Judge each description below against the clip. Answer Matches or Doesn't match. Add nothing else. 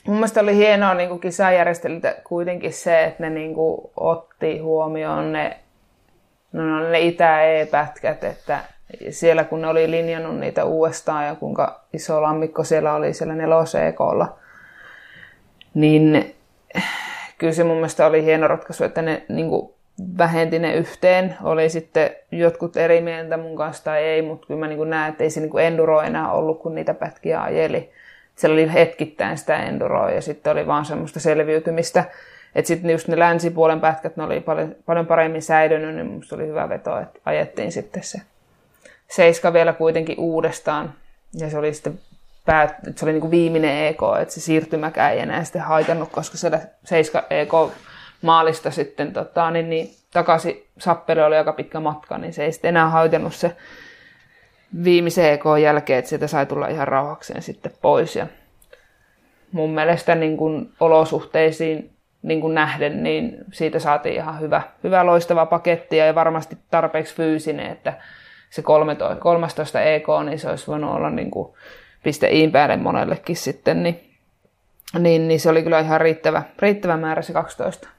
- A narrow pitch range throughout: Matches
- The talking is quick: Matches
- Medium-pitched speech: Matches